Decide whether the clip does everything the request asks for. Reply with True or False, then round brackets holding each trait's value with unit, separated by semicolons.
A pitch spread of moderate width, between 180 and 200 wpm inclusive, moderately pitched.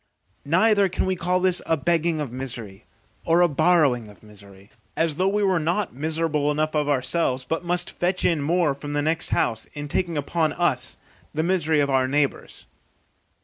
True (3.9 semitones; 185 wpm; 155 Hz)